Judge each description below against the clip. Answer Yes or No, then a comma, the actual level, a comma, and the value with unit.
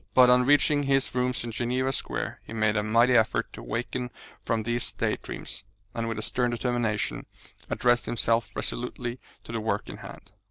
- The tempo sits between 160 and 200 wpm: Yes, average, 185 wpm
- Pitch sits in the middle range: No, low, 120 Hz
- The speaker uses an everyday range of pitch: No, narrow, 1.9 semitones